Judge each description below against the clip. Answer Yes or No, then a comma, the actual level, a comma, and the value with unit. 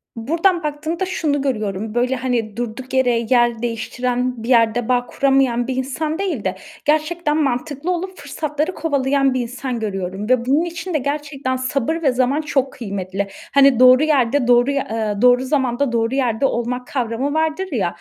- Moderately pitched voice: No, very high, 260 Hz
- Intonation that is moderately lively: Yes, average, 3.6 semitones